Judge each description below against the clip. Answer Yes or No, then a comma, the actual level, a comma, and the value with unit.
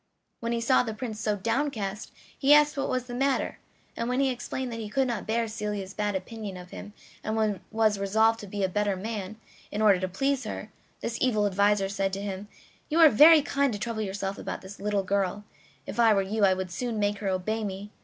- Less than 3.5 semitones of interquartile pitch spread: Yes, average, 2.9 semitones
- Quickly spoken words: Yes, fast, 225 wpm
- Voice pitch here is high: Yes, high, 215 Hz